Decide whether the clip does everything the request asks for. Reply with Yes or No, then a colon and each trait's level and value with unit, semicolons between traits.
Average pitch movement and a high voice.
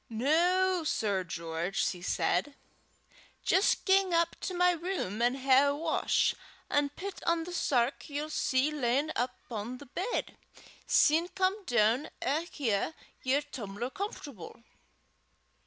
No: wide, 6.4 semitones; very high, 285 Hz